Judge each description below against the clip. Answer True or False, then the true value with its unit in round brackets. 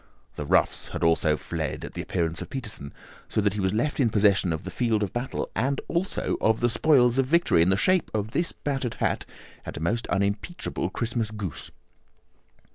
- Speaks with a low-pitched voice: True (110 Hz)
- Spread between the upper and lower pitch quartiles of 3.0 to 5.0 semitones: False (5.4 semitones)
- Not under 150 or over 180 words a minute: False (200 wpm)